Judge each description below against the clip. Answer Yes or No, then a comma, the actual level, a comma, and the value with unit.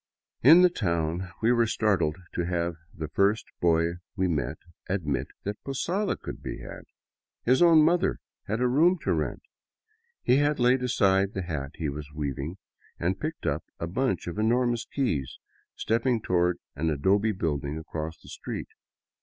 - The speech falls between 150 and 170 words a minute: Yes, average, 160 wpm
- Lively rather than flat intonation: Yes, wide, 7.2 semitones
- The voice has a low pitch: Yes, very low, 95 Hz